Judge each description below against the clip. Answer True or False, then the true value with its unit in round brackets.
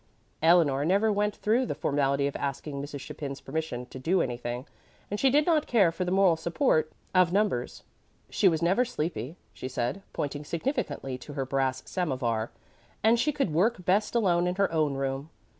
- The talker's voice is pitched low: False (160 Hz)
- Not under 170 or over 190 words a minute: True (180 wpm)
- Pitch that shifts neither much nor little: False (6.3 semitones)